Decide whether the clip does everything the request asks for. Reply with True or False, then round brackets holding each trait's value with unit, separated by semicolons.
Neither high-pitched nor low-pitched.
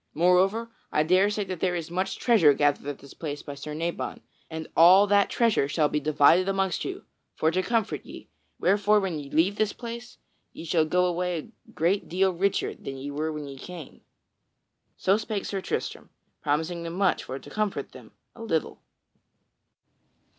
True (180 Hz)